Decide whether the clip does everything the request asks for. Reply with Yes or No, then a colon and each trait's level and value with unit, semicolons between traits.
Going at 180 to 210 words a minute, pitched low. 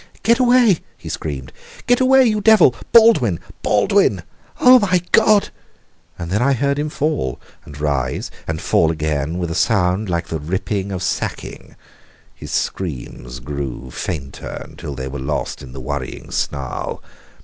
No: average, 150 wpm; very low, 85 Hz